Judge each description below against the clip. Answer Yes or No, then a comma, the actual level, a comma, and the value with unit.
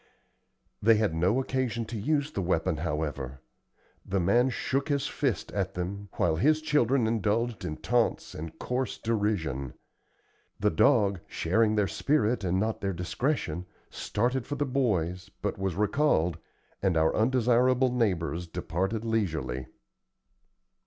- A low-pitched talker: Yes, low, 105 Hz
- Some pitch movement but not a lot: No, wide, 6.1 semitones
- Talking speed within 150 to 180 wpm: No, slow, 135 wpm